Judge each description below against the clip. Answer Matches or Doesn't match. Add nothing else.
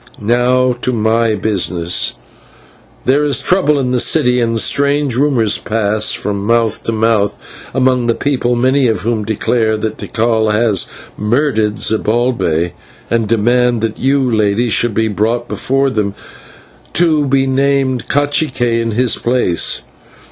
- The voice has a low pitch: Matches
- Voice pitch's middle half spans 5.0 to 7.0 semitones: Doesn't match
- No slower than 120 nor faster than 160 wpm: Matches